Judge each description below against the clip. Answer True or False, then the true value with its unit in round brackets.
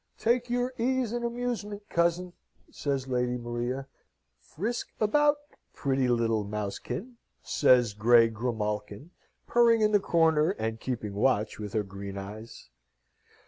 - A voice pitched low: True (130 Hz)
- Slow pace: True (125 wpm)